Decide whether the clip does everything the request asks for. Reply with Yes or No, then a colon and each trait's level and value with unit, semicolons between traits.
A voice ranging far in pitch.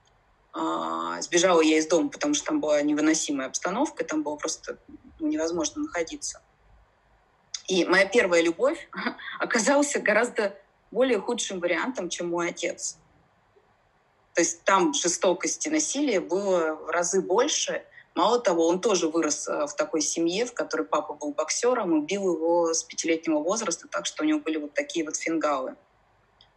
Yes: wide, 7.5 semitones